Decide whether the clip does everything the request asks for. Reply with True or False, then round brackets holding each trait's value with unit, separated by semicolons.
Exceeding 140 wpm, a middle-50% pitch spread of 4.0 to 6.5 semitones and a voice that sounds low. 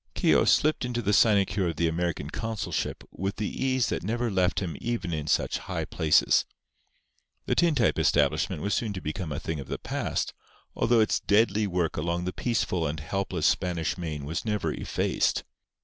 True (180 wpm; 5.0 semitones; 95 Hz)